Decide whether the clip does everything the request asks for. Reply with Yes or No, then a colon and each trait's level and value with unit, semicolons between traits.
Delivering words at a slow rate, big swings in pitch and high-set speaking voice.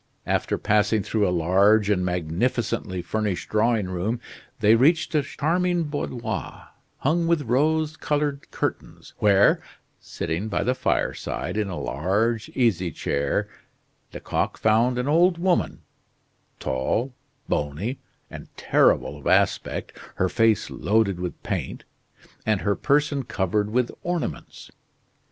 No: slow, 125 wpm; wide, 6.8 semitones; low, 110 Hz